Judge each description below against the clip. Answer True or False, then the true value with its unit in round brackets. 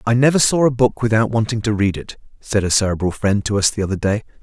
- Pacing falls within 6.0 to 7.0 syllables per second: True (6.4 syllables/s)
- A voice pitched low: True (110 Hz)